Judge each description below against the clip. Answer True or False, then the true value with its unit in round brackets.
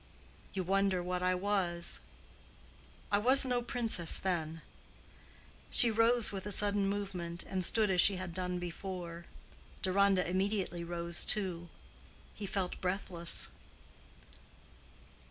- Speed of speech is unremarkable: False (120 wpm)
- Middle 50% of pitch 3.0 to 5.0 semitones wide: False (2.6 semitones)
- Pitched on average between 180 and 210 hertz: True (185 Hz)